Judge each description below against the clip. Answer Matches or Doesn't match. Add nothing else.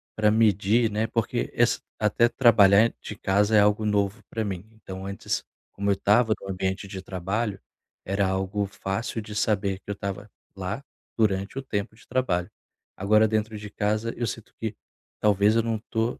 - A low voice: Matches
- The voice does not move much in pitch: Matches